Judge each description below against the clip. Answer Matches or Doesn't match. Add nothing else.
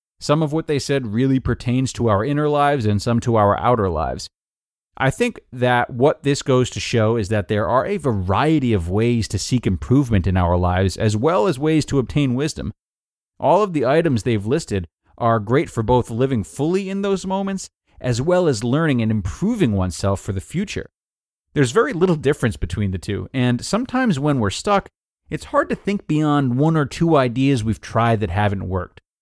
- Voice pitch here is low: Matches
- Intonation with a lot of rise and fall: Matches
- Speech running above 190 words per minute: Matches